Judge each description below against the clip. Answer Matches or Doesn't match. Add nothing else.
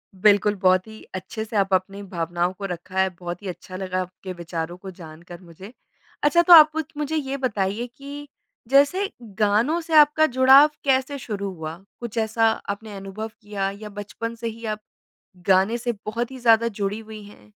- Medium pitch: Doesn't match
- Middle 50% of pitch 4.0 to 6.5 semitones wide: Matches